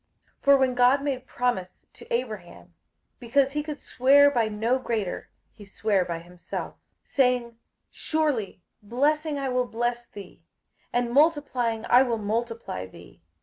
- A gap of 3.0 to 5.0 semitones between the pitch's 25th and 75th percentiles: Yes, average, 3.8 semitones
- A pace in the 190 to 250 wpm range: No, average, 145 wpm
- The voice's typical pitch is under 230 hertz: No, high, 245 Hz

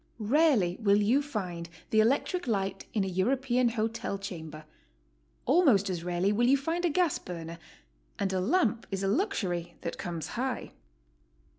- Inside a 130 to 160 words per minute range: Yes, average, 155 wpm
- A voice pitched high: Yes, high, 210 Hz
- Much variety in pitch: Yes, wide, 6.5 semitones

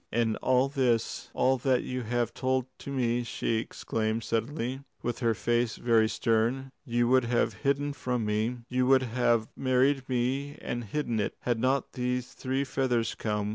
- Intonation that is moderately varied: No, narrow, 2.1 semitones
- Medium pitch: No, low, 125 Hz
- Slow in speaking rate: No, average, 170 wpm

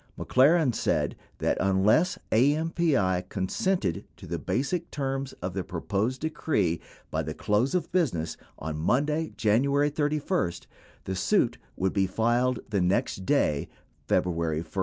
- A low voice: Yes, low, 120 Hz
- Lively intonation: Yes, wide, 8.0 semitones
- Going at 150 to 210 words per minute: No, slow, 135 wpm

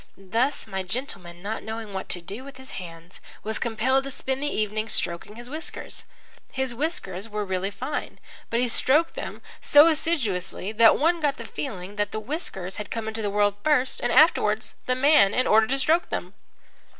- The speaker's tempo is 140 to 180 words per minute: No, average, 190 wpm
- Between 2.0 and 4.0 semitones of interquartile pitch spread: No, average, 5.2 semitones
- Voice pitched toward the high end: Yes, high, 225 Hz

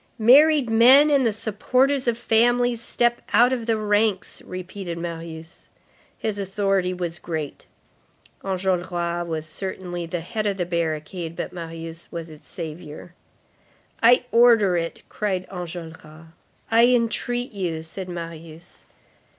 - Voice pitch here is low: No, medium, 185 Hz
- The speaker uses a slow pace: Yes, slow, 125 wpm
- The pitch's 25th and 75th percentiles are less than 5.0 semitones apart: No, average, 5.3 semitones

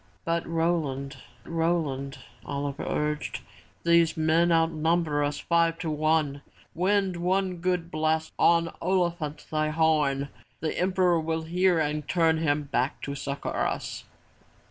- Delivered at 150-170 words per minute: No, slow, 135 wpm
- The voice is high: No, medium, 160 Hz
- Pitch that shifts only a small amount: Yes, narrow, 2.2 semitones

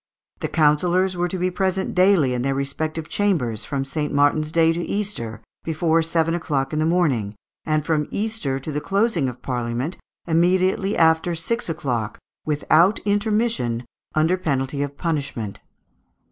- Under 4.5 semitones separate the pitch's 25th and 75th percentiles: No, average, 4.8 semitones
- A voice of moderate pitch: Yes, medium, 160 Hz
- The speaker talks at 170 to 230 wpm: No, average, 150 wpm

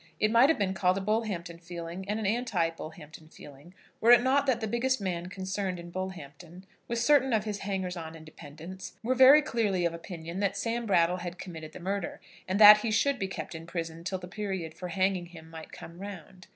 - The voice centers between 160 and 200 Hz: Yes, medium, 185 Hz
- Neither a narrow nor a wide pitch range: Yes, average, 4.0 semitones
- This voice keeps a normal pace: No, fast, 215 wpm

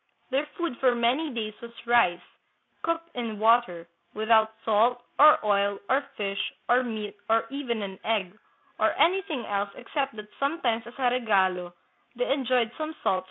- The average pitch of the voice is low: No, high, 235 Hz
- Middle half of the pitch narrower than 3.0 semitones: No, average, 4.1 semitones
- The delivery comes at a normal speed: Yes, average, 160 wpm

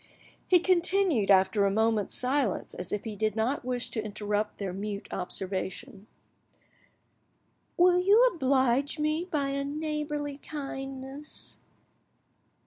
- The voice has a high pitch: Yes, very high, 265 Hz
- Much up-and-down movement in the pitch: Yes, wide, 6.3 semitones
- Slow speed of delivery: Yes, slow, 120 wpm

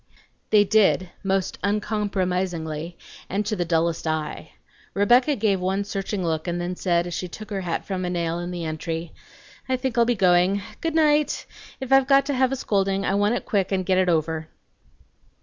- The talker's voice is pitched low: No, high, 190 Hz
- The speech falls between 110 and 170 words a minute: No, average, 195 wpm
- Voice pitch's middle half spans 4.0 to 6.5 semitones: No, average, 3.5 semitones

